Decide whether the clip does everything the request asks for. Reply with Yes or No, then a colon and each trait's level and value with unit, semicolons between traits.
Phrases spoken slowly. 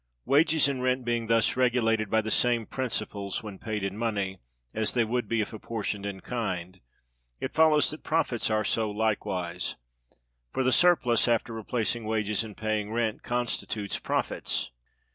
No: average, 160 wpm